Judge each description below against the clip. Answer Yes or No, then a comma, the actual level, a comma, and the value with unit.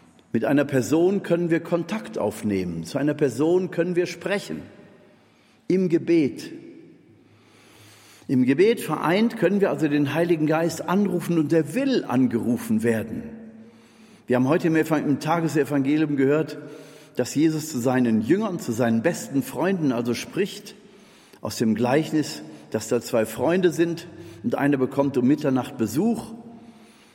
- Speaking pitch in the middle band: Yes, medium, 155 Hz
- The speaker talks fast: No, average, 135 wpm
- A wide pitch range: Yes, wide, 5.9 semitones